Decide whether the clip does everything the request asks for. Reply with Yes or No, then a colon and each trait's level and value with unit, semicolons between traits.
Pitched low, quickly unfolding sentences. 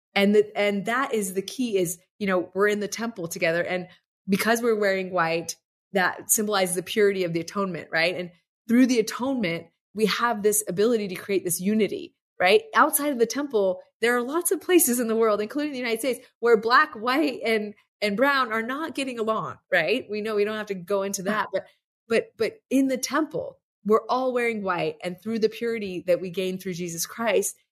No: high, 215 Hz; fast, 210 wpm